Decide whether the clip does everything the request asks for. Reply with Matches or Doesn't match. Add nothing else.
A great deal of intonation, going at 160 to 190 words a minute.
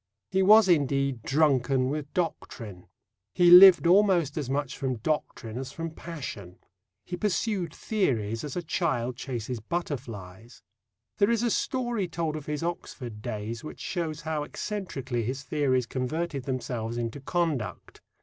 Doesn't match